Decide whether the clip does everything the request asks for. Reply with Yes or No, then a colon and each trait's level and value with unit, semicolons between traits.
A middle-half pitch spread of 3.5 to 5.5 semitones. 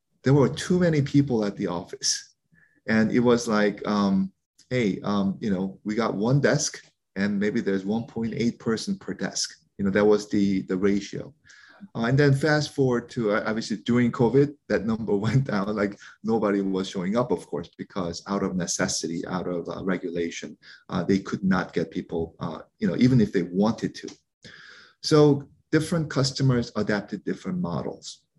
Yes: average, 4.7 semitones